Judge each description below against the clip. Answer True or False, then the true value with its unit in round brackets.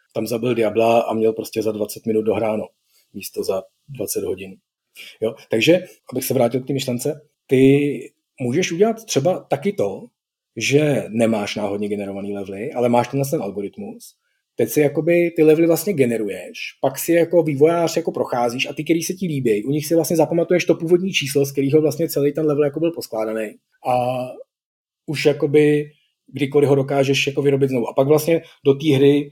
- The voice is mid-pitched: True (145 Hz)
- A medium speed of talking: False (180 wpm)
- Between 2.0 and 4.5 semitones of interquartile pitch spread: False (4.9 semitones)